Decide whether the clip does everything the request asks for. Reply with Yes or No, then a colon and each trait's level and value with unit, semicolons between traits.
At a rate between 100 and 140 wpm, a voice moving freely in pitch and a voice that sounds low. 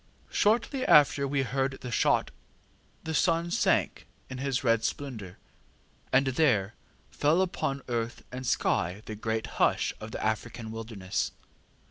No: slow, 135 wpm; average, 4.3 semitones; low, 125 Hz